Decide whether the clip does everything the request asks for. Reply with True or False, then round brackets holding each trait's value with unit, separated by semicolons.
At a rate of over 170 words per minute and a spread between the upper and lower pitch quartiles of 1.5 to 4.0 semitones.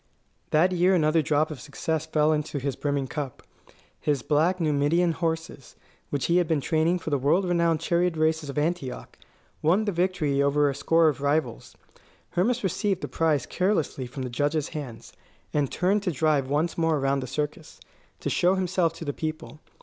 True (180 wpm; 3.1 semitones)